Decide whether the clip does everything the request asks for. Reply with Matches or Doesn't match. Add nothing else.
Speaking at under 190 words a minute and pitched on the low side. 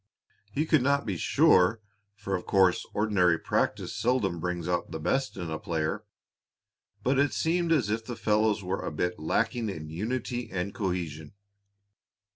Matches